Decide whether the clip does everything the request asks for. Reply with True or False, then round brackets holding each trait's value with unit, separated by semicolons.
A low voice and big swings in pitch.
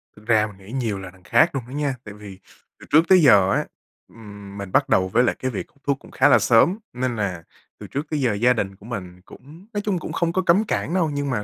True (120 Hz; 6.5 semitones)